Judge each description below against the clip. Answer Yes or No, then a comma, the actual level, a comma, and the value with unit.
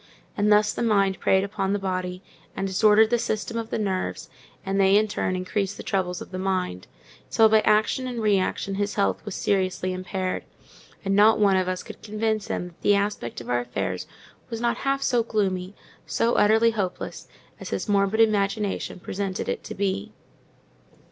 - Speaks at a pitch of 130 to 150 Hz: No, high, 200 Hz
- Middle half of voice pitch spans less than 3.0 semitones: Yes, narrow, 2.5 semitones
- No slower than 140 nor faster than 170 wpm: No, average, 185 wpm